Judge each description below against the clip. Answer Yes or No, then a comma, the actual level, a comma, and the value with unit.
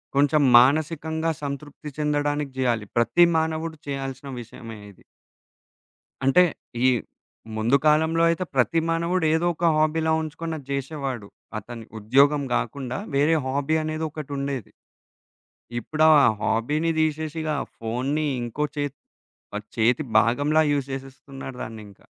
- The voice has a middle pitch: Yes, medium, 145 Hz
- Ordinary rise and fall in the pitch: Yes, average, 3.4 semitones